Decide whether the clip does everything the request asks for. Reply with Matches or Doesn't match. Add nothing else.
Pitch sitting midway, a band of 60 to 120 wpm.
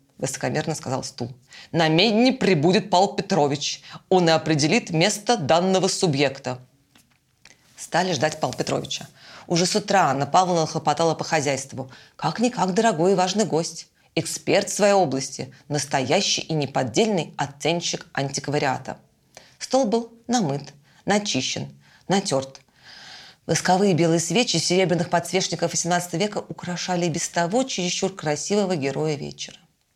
Matches